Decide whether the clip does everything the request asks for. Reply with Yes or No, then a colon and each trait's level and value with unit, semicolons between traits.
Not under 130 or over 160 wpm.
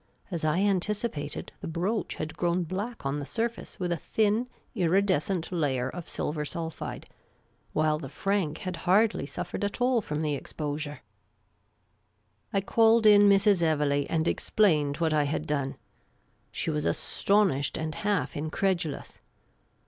Yes: average, 145 wpm